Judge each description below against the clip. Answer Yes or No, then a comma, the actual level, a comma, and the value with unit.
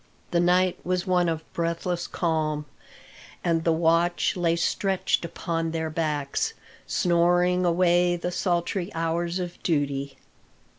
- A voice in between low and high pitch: Yes, medium, 170 Hz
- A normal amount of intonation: No, narrow, 1.4 semitones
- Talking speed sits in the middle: No, slow, 120 wpm